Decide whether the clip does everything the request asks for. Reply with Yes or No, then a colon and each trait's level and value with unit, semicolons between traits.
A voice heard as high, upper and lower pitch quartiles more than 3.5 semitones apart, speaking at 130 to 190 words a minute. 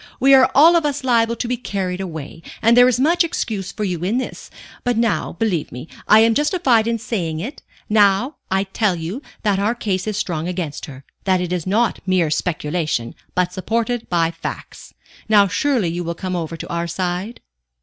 No: high, 195 Hz; average, 5.1 semitones; average, 200 wpm